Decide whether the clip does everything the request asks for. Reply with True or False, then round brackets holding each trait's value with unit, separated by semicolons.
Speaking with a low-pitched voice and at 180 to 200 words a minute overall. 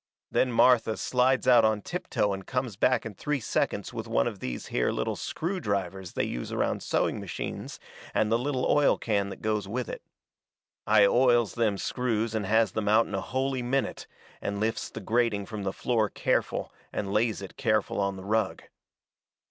True (110 Hz; 190 wpm)